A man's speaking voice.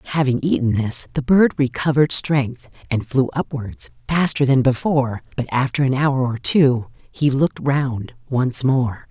No: female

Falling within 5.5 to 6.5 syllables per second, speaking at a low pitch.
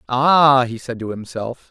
No: 3.9 syllables/s; low, 125 Hz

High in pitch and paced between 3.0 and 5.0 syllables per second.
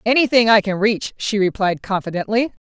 No: high, 210 Hz; 5.4 syllables/s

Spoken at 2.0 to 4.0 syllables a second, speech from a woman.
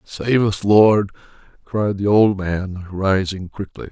No: 3.4 syllables/s; male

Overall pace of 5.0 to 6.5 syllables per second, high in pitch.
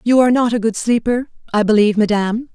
No: 6.8 syllables/s; high, 225 Hz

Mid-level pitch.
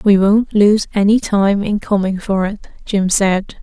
No: high, 200 Hz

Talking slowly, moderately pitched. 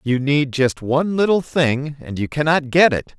No: fast, 205 wpm; medium, 145 Hz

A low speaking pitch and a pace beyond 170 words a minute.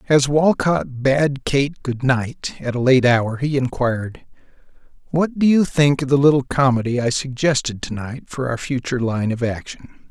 Yes: low, 130 Hz; average, 180 wpm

